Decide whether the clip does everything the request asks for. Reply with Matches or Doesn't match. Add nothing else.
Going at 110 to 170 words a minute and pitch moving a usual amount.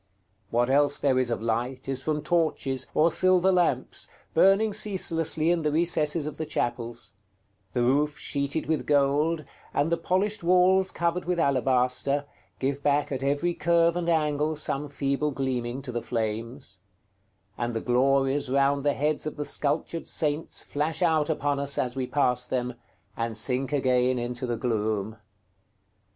Matches